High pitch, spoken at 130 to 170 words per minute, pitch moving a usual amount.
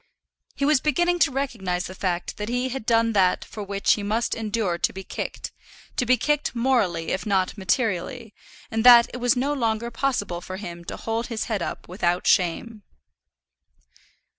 No: high, 225 Hz; average, 180 wpm; average, 4.7 semitones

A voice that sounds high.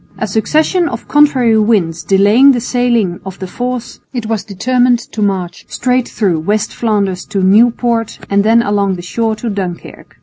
Yes: high, 220 Hz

